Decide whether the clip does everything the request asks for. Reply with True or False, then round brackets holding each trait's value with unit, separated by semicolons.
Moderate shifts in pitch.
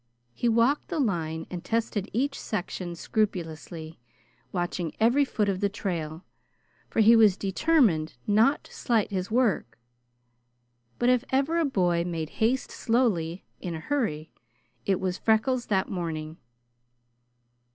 False (5.7 semitones)